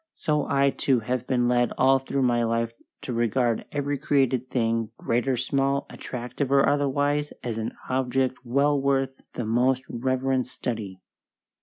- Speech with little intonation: Yes, narrow, 2.3 semitones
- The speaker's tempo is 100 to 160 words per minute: Yes, average, 155 wpm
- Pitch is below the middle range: Yes, low, 130 Hz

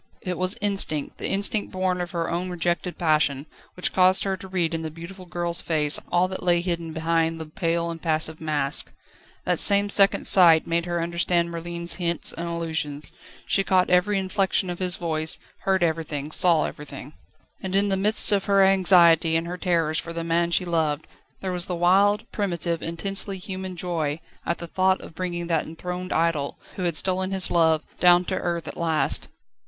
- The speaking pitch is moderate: Yes, medium, 175 Hz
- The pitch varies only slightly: Yes, narrow, 2.2 semitones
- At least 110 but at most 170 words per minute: No, average, 190 wpm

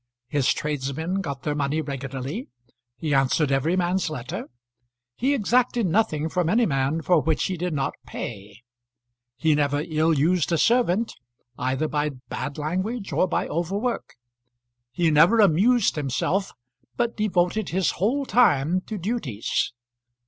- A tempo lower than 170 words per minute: Yes, average, 140 wpm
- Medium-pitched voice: Yes, medium, 165 Hz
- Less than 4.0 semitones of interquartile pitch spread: No, wide, 5.5 semitones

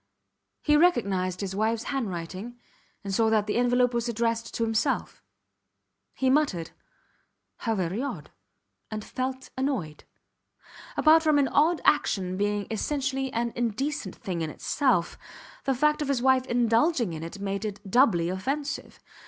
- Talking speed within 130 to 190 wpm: Yes, average, 145 wpm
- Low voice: No, high, 235 Hz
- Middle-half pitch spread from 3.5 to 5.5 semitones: Yes, average, 5.2 semitones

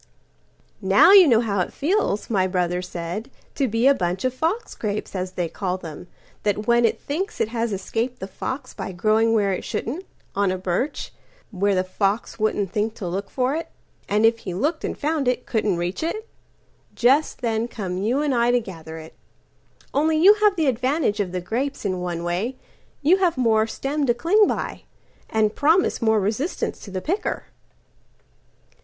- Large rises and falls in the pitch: Yes, wide, 6.4 semitones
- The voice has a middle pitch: No, high, 225 Hz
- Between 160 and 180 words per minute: Yes, average, 170 wpm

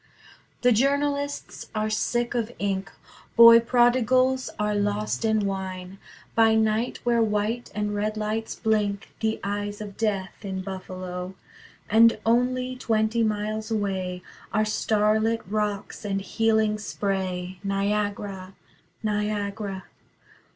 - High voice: Yes, high, 215 Hz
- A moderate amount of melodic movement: No, narrow, 2.2 semitones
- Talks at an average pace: No, slow, 115 wpm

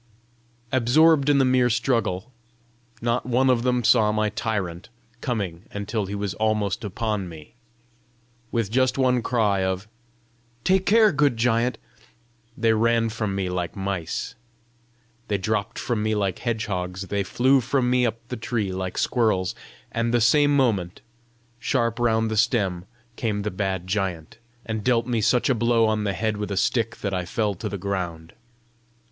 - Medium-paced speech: Yes, average, 165 wpm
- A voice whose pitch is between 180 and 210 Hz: No, low, 110 Hz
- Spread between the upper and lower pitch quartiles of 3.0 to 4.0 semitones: Yes, average, 3.7 semitones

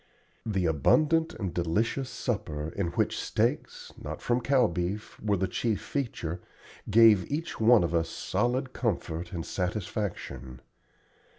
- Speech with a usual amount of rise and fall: No, wide, 5.9 semitones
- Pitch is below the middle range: Yes, low, 100 Hz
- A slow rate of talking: Yes, slow, 130 wpm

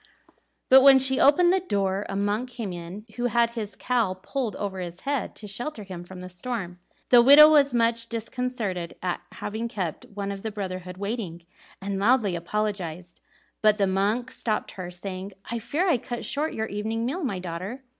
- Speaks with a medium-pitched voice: No, high, 210 Hz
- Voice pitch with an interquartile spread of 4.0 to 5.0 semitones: Yes, average, 4.5 semitones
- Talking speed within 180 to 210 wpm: Yes, average, 185 wpm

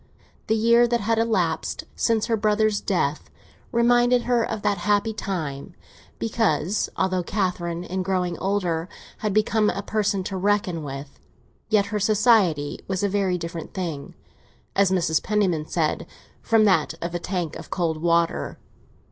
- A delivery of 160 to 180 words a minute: No, average, 150 wpm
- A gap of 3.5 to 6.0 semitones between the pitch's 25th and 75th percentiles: Yes, average, 4.0 semitones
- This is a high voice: Yes, high, 195 Hz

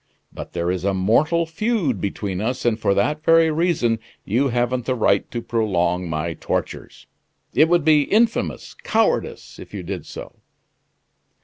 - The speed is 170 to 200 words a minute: No, average, 155 wpm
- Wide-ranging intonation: Yes, wide, 8.4 semitones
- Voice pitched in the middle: No, low, 120 Hz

